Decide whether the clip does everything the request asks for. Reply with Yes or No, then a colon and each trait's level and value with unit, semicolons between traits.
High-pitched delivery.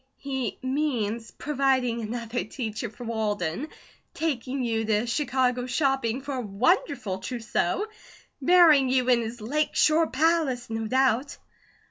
Yes: very high, 250 Hz